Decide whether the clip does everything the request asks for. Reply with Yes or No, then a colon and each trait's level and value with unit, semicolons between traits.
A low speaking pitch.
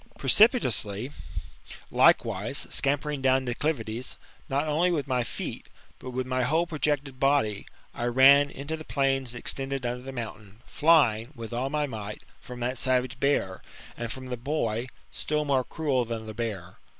Yes: low, 130 Hz